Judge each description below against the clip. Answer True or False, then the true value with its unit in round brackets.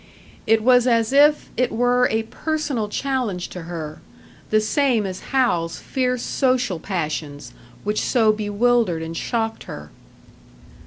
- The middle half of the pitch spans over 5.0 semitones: True (5.6 semitones)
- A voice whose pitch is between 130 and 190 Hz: False (225 Hz)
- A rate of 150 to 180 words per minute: False (135 wpm)